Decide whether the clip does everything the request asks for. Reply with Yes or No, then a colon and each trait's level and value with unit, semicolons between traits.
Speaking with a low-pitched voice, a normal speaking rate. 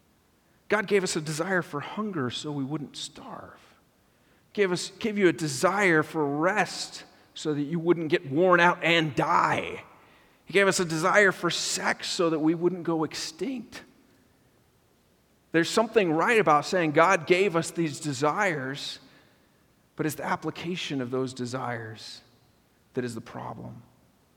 No: medium, 165 Hz; average, 155 wpm